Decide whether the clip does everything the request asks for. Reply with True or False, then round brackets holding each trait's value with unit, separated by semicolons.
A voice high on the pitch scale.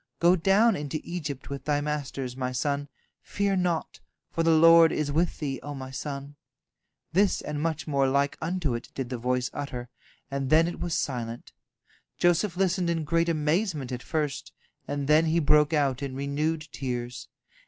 False (150 Hz)